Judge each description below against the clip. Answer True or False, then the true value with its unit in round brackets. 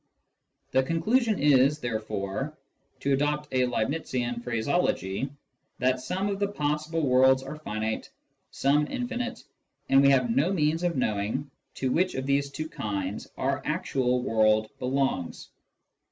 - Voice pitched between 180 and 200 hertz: False (135 Hz)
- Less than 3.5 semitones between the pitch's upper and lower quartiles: False (4.0 semitones)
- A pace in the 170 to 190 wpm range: False (135 wpm)